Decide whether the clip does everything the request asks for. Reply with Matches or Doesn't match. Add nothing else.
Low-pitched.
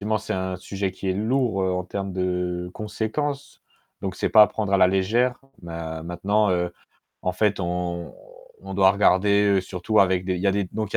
Matches